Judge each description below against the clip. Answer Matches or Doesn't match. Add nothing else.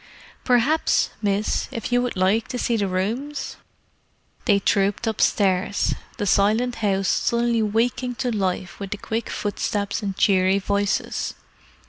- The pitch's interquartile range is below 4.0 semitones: Matches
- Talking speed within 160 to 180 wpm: Doesn't match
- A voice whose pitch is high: Matches